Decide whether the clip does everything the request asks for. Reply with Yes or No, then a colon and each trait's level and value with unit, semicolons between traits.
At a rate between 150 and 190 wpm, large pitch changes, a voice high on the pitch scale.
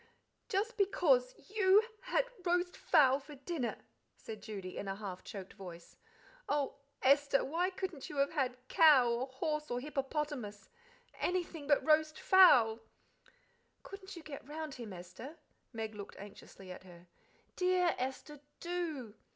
No: average, 140 wpm; wide, 7.1 semitones; very high, 280 Hz